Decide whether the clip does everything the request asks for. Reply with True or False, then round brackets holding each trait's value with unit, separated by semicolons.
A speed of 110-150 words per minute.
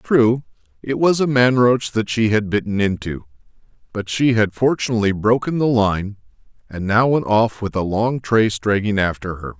False (180 wpm)